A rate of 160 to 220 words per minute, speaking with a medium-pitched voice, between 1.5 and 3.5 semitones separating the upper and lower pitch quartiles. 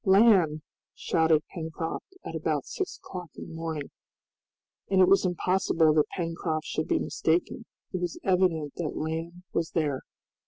No: average, 150 wpm; medium, 165 Hz; narrow, 2.5 semitones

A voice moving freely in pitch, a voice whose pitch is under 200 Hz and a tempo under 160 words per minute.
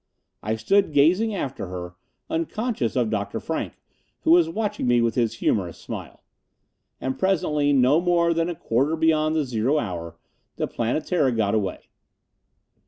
Yes: wide, 6.7 semitones; medium, 140 Hz; average, 150 wpm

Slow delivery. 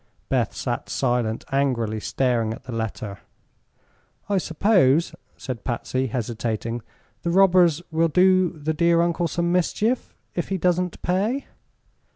Yes: slow, 130 wpm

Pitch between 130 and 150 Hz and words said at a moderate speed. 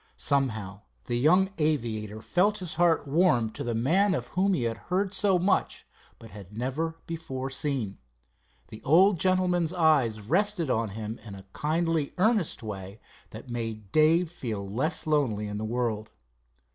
Yes: medium, 140 Hz; average, 160 wpm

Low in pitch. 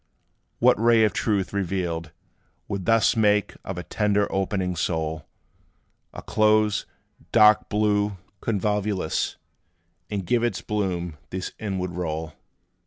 Yes: low, 100 Hz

